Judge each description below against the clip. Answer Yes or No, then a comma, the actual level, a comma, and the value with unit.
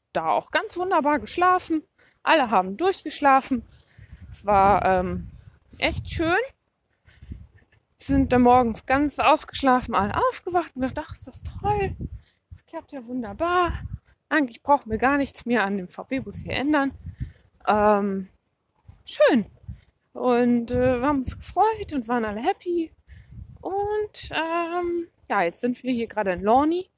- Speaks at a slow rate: No, average, 140 wpm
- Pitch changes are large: Yes, wide, 5.9 semitones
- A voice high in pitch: Yes, very high, 275 Hz